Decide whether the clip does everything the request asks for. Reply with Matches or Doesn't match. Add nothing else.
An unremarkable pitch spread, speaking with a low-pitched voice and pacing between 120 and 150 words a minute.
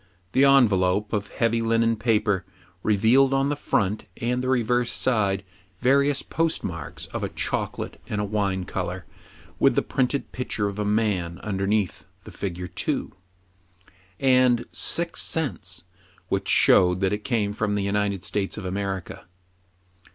Matches